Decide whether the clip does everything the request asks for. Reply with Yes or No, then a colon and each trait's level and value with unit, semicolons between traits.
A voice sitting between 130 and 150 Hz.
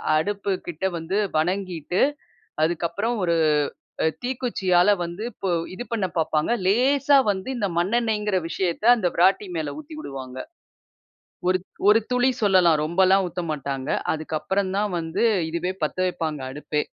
No: medium, 185 Hz